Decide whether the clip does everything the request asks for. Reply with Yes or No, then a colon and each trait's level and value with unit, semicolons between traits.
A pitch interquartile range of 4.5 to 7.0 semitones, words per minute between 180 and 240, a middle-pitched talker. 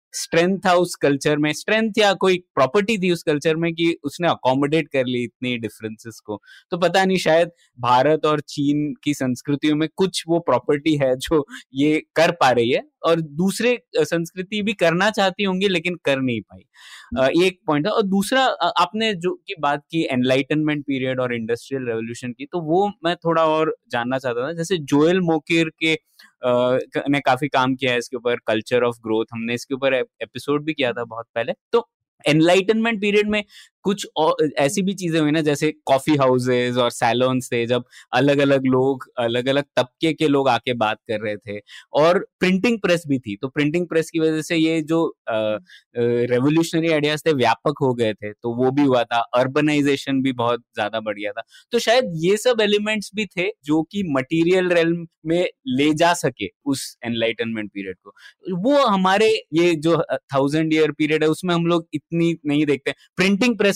Yes: wide, 5.4 semitones; average, 185 wpm; medium, 150 Hz